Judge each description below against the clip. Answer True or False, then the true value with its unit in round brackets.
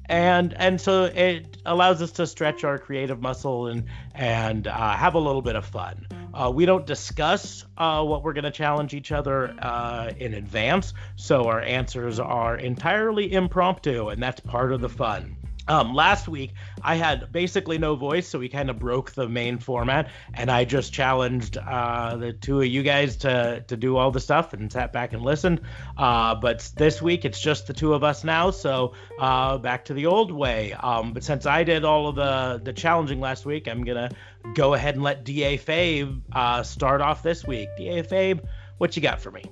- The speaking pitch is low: True (130 Hz)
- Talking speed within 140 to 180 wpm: False (205 wpm)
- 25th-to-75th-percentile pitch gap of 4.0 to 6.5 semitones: True (4.3 semitones)